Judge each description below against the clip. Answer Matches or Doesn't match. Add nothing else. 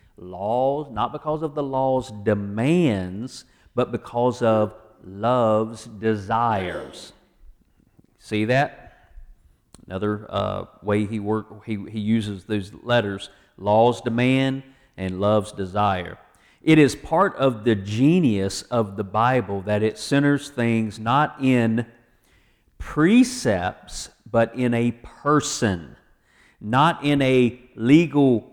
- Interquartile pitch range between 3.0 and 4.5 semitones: Matches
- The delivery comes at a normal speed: Doesn't match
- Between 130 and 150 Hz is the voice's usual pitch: Doesn't match